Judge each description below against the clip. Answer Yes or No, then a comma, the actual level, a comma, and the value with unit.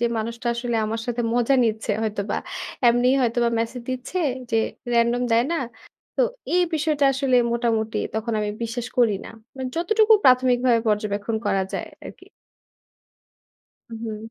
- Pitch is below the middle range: No, high, 235 Hz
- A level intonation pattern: Yes, narrow, 2.2 semitones